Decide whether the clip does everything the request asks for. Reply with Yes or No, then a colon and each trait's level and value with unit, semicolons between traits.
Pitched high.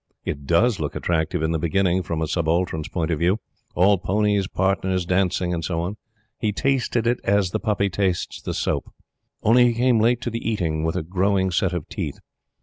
No: very low, 95 Hz